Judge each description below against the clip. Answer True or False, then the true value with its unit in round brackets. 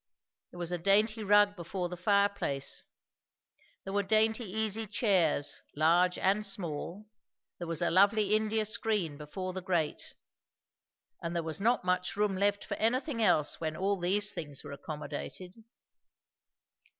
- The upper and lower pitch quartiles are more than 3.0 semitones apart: True (3.6 semitones)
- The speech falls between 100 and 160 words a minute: True (145 wpm)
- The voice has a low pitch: False (190 Hz)